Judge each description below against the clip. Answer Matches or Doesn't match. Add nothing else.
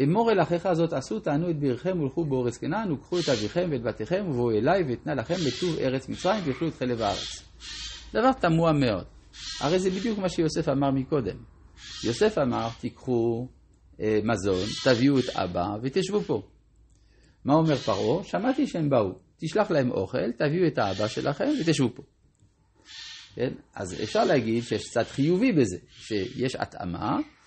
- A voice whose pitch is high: Doesn't match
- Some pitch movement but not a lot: Doesn't match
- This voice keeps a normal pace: Doesn't match